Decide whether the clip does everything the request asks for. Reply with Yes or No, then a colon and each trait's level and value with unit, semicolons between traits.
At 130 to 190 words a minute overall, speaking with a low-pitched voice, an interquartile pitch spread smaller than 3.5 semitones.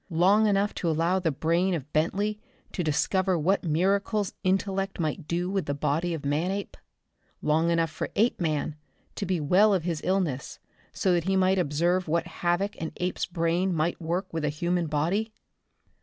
No: average, 170 wpm; medium, 175 Hz; average, 3.1 semitones